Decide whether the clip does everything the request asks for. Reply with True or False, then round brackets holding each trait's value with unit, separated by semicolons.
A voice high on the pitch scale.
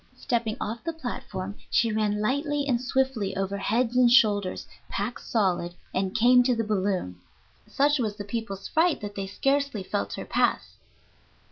True (220 Hz)